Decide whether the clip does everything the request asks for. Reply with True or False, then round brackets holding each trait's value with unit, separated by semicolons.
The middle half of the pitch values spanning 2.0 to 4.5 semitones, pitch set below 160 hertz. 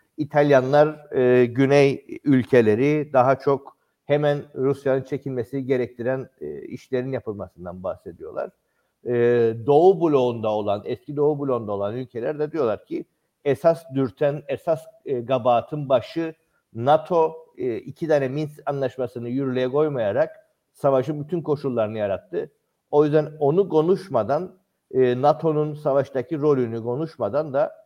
True (3.3 semitones; 140 Hz)